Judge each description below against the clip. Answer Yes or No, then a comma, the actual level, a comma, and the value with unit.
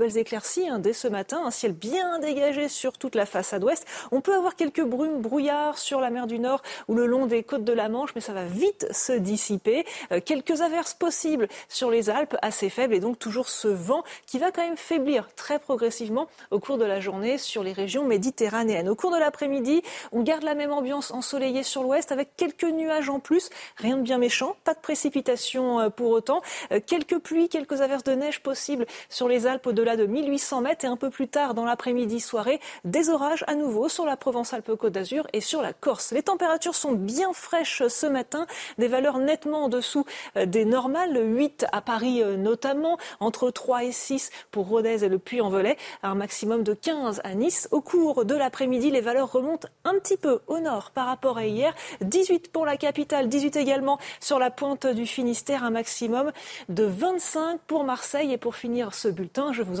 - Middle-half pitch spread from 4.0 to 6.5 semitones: Yes, average, 4.4 semitones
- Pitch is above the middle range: Yes, very high, 265 Hz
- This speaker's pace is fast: No, average, 205 wpm